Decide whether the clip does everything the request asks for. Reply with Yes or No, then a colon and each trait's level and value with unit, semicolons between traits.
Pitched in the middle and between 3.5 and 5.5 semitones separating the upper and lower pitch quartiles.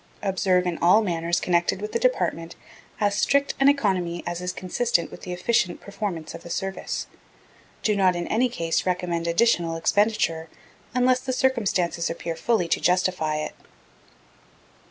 Yes: medium, 180 Hz; average, 4.0 semitones